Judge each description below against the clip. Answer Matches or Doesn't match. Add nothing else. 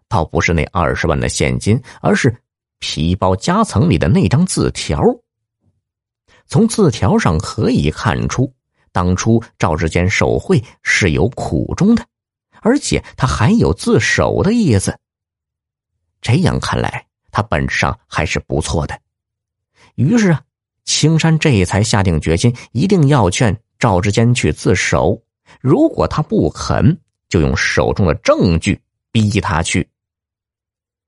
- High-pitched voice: Doesn't match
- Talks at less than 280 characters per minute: Matches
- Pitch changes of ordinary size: Doesn't match